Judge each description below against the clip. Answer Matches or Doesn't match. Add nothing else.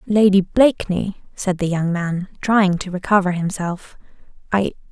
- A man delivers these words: Doesn't match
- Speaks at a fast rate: Doesn't match